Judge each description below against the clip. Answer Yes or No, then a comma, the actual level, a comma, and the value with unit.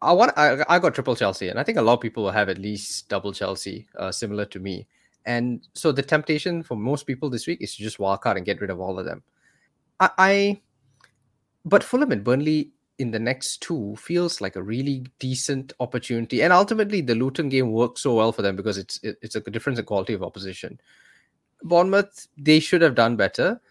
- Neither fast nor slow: No, fast, 220 wpm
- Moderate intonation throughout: No, wide, 6.5 semitones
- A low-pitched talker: Yes, low, 120 Hz